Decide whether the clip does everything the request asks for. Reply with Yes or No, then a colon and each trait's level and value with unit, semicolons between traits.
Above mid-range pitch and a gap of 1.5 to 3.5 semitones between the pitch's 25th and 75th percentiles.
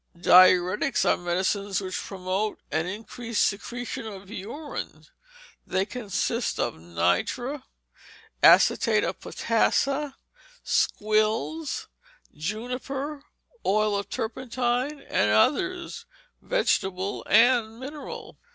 No: high, 215 Hz; wide, 5.4 semitones